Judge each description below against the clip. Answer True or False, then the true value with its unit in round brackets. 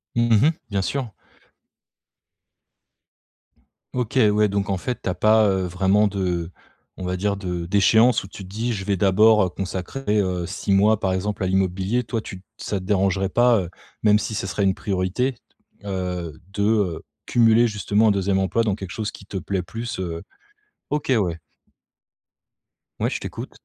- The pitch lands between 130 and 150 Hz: False (100 Hz)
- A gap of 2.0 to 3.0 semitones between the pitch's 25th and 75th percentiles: True (2.7 semitones)